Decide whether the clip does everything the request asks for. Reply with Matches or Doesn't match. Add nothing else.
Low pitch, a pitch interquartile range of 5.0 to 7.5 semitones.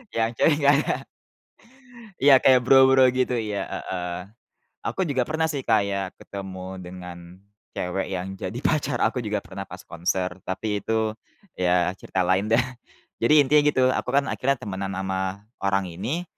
Matches